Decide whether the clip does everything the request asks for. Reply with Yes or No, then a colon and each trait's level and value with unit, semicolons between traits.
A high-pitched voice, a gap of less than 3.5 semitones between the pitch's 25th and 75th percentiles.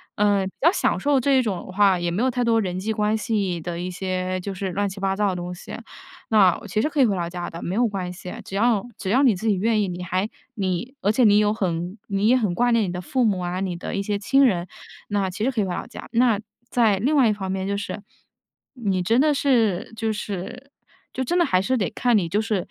No: high, 205 Hz; average, 3.8 semitones